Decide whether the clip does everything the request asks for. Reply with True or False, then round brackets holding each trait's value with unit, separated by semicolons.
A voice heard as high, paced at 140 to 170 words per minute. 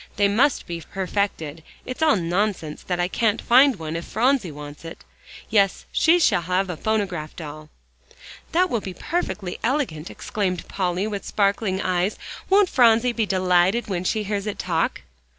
True (195 Hz; 165 wpm)